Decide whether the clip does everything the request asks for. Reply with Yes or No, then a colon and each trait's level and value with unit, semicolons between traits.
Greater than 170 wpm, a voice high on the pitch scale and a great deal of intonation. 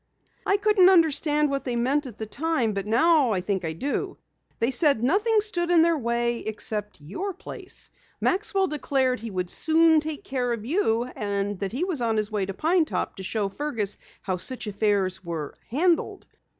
Yes: average, 190 wpm; very high, 250 Hz; wide, 7.5 semitones